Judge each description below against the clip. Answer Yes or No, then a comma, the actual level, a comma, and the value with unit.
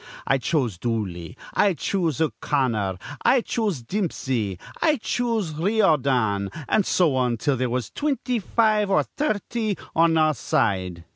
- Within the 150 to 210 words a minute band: No, slow, 135 wpm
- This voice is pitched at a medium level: Yes, medium, 150 Hz